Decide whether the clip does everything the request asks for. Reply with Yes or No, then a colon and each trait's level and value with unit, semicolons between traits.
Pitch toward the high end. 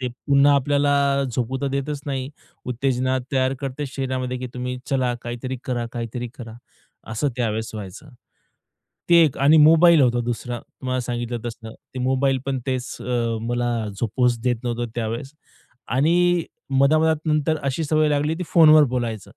No: low, 130 Hz